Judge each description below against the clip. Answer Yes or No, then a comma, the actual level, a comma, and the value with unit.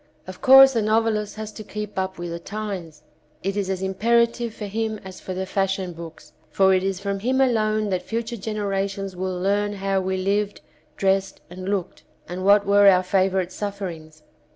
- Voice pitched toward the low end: No, high, 195 Hz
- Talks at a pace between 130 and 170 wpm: No, average, 185 wpm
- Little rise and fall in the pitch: Yes, narrow, 2.2 semitones